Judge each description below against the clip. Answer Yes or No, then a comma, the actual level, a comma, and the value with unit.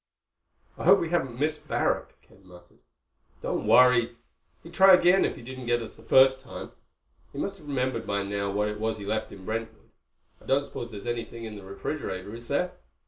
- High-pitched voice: No, low, 120 Hz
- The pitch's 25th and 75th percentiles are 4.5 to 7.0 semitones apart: Yes, average, 5.1 semitones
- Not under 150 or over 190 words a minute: No, average, 200 wpm